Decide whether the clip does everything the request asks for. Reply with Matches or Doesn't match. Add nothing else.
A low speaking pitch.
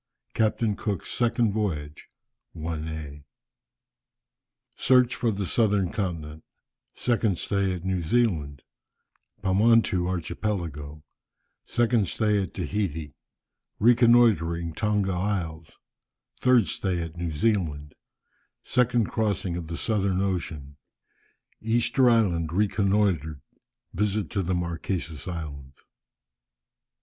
Matches